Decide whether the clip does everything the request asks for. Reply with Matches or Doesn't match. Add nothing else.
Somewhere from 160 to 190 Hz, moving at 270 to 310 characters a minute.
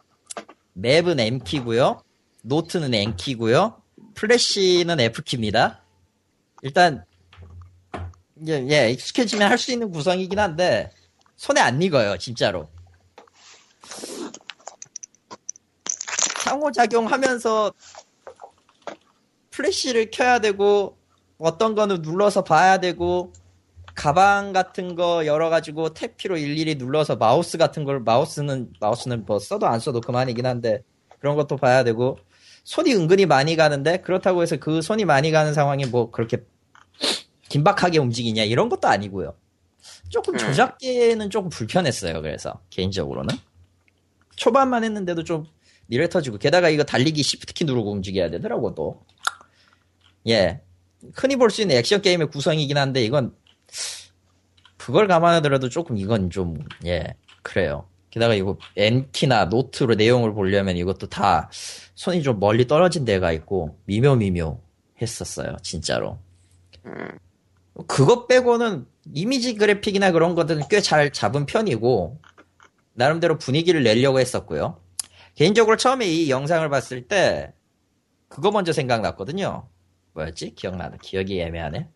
Doesn't match